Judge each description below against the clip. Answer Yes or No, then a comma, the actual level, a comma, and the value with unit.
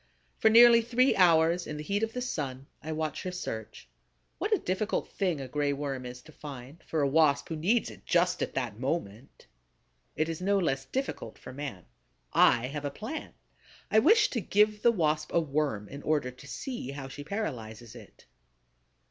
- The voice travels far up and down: Yes, wide, 6.8 semitones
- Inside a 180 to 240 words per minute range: Yes, average, 190 wpm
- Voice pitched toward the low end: No, medium, 155 Hz